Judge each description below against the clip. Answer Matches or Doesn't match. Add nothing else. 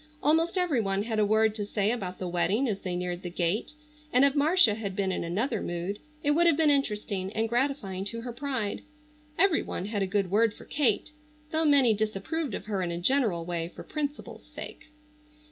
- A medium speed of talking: Doesn't match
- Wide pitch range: Matches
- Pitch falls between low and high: Doesn't match